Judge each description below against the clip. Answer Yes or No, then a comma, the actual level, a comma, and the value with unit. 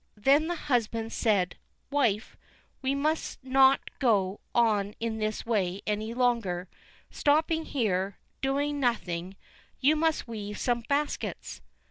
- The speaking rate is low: Yes, slow, 120 wpm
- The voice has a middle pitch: No, high, 235 Hz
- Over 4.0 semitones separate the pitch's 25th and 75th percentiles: Yes, average, 5.1 semitones